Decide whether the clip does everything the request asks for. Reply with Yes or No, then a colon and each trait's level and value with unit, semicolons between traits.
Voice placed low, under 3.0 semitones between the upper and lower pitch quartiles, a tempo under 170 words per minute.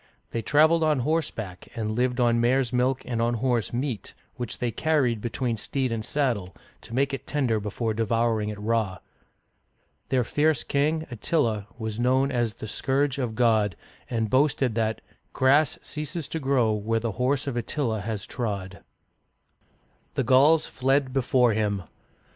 No: low, 120 Hz; average, 3.6 semitones; average, 160 wpm